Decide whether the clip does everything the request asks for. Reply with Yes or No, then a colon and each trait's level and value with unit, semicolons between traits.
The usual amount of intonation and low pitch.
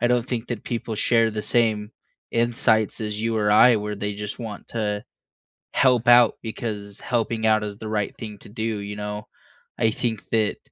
No: narrow, 1.9 semitones; low, 110 Hz